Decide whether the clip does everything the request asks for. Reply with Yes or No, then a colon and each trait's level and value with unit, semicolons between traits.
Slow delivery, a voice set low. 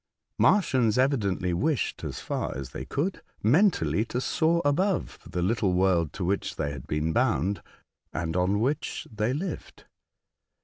No: average, 150 wpm; low, 105 Hz